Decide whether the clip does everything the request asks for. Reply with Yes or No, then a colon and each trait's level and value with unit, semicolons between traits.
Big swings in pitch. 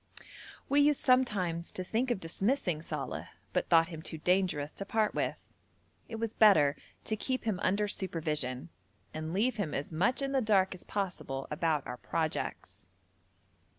Yes: wide, 5.7 semitones